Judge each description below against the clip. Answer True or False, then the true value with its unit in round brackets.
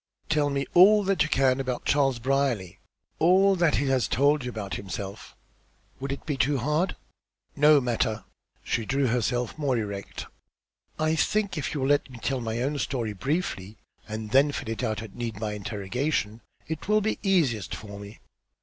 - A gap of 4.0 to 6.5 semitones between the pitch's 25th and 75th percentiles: True (5.2 semitones)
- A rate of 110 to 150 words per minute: False (180 wpm)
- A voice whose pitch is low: True (130 Hz)